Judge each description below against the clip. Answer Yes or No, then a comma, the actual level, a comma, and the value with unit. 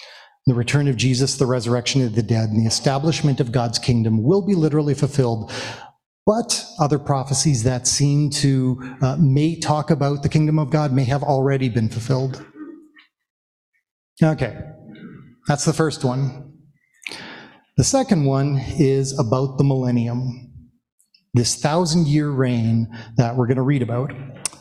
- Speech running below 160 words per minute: Yes, average, 145 wpm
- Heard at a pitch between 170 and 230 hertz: No, low, 135 Hz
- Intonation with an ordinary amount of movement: Yes, average, 3.1 semitones